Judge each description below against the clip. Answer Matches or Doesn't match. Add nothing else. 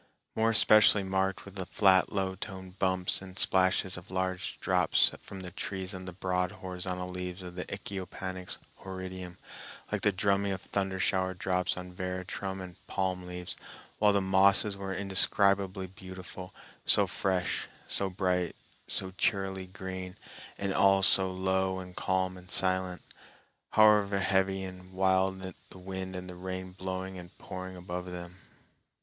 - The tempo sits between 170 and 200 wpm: Doesn't match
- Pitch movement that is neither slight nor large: Doesn't match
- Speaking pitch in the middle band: Doesn't match